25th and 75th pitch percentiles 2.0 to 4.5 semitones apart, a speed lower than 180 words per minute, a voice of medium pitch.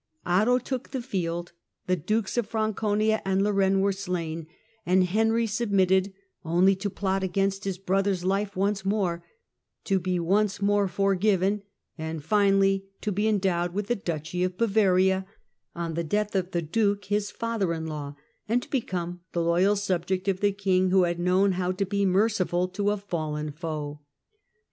No: narrow, 2.4 semitones; average, 170 wpm; high, 195 Hz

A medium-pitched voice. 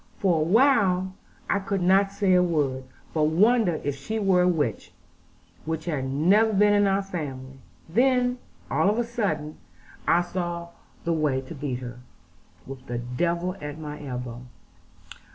Yes: medium, 170 Hz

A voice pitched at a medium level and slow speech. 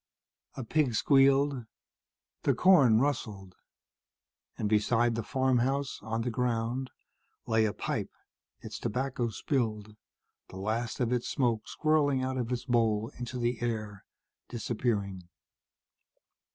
No: low, 120 Hz; slow, 120 wpm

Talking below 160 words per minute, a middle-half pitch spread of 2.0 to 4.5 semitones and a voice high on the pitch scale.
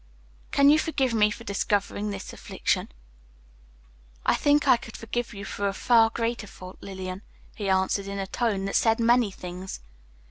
No: average, 165 wpm; average, 3.2 semitones; high, 210 Hz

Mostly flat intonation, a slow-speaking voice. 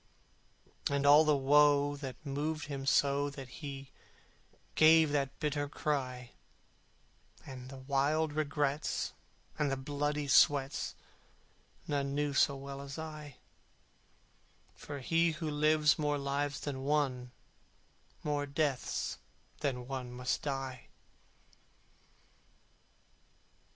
Yes: narrow, 1.5 semitones; slow, 105 wpm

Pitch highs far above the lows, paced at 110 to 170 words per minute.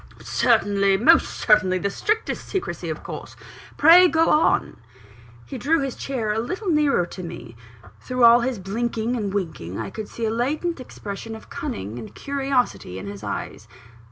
Yes: wide, 6.3 semitones; average, 165 wpm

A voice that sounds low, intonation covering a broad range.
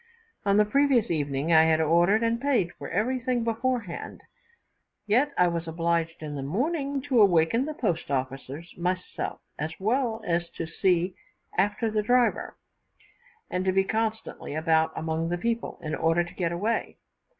No: medium, 185 Hz; wide, 5.9 semitones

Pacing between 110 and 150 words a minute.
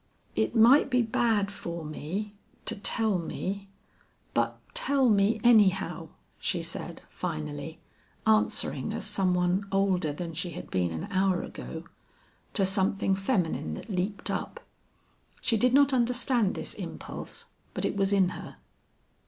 Yes: average, 140 wpm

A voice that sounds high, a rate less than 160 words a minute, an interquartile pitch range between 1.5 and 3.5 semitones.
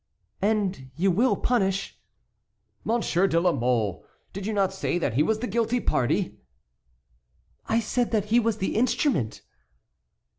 No: high, 195 Hz; average, 145 wpm; average, 5.0 semitones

